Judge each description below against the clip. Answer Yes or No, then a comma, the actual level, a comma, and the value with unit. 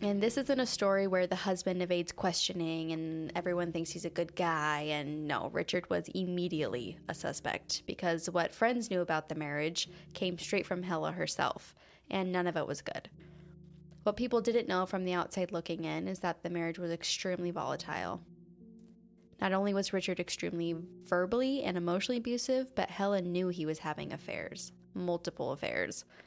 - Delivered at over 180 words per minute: No, average, 175 wpm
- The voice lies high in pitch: No, medium, 175 Hz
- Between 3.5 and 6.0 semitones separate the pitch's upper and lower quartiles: No, narrow, 2.4 semitones